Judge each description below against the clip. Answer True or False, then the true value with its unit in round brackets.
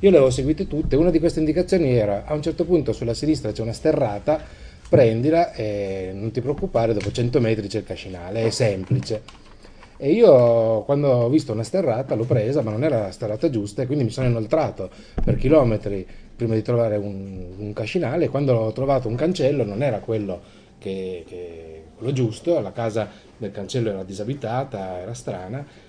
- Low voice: True (115 Hz)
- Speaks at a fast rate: True (190 wpm)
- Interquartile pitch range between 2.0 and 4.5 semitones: False (5.2 semitones)